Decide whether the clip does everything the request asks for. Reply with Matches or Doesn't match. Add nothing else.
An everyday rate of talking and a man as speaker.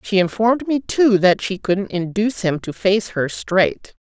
Doesn't match